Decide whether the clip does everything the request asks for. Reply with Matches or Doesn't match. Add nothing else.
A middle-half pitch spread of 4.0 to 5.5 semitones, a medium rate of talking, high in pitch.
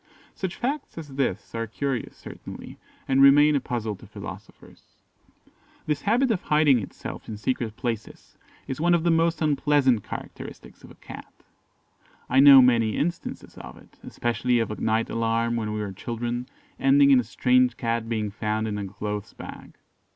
Doesn't match